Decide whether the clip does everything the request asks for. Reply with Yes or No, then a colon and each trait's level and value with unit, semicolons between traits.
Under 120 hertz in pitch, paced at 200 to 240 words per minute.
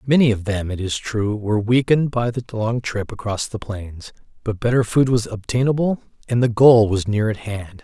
Yes: low, 110 Hz; fast, 205 wpm